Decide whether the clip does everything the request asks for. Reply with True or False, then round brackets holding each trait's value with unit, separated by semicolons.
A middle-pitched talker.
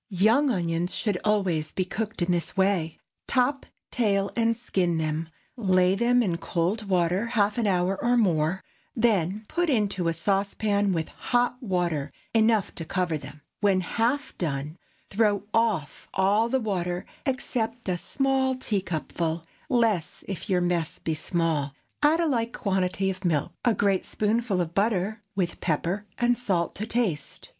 False (195 Hz)